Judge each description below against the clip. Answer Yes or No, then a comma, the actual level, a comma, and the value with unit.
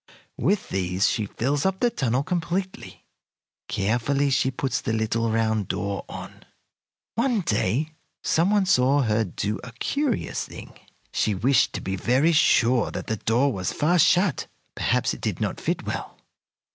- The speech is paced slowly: No, average, 160 wpm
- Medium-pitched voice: No, low, 130 Hz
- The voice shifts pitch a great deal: Yes, wide, 7.3 semitones